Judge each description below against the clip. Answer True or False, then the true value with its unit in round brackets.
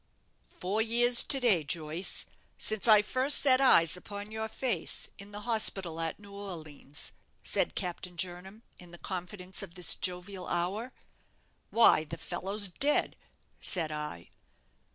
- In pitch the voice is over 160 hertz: True (190 Hz)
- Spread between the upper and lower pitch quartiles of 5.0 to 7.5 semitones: False (4.0 semitones)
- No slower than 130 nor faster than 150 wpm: True (140 wpm)